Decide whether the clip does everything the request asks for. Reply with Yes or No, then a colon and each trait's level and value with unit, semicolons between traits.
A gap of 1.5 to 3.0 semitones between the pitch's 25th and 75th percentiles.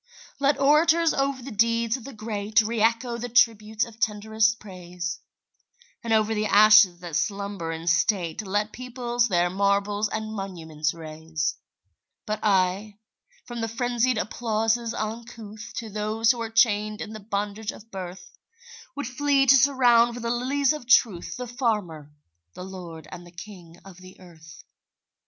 No: average, 3.9 semitones